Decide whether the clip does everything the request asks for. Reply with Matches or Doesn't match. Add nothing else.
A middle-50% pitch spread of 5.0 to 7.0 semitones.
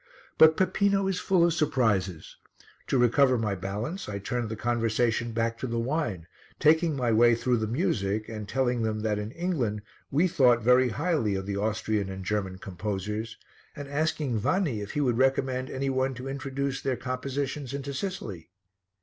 Doesn't match